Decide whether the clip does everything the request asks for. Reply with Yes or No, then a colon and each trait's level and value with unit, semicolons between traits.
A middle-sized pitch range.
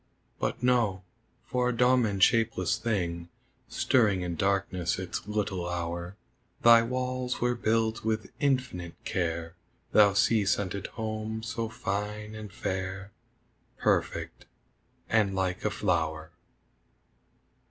Yes: average, 3.6 semitones